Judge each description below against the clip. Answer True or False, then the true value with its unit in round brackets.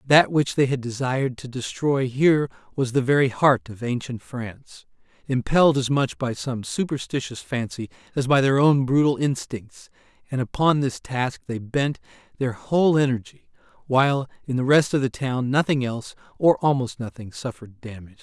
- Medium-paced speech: True (170 wpm)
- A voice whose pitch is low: True (130 Hz)